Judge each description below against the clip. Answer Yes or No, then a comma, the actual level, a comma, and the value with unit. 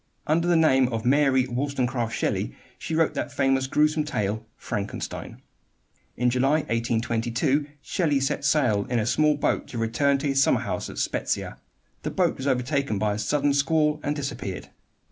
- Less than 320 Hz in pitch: Yes, low, 135 Hz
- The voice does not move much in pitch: No, average, 3.9 semitones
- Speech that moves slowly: No, average, 165 wpm